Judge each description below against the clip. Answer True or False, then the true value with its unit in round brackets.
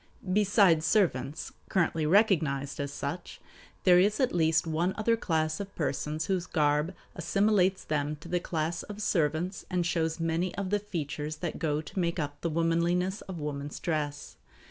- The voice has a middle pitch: True (165 Hz)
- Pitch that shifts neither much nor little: True (3.5 semitones)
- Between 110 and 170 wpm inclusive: True (165 wpm)